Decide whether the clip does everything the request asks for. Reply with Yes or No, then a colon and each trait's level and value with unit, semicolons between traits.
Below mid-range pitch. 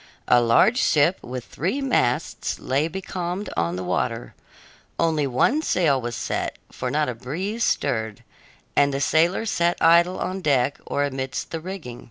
No: medium, 145 Hz